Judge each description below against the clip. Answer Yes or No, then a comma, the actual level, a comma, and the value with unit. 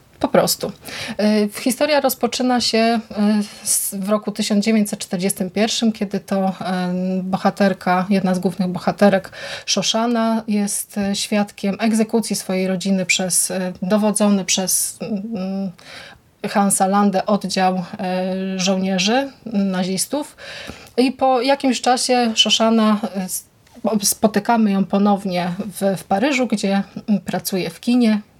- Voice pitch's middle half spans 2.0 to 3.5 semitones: Yes, average, 2.7 semitones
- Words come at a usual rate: No, slow, 95 wpm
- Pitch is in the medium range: No, high, 205 Hz